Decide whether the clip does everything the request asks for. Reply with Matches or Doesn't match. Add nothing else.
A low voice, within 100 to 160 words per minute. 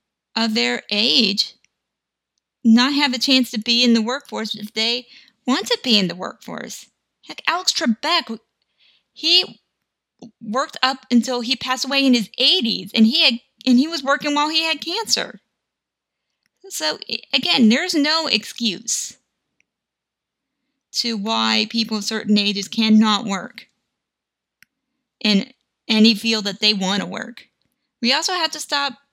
Doesn't match